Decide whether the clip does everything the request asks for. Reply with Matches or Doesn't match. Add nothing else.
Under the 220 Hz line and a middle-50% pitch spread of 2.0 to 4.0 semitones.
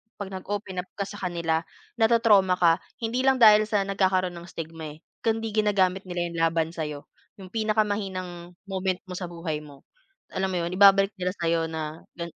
Matches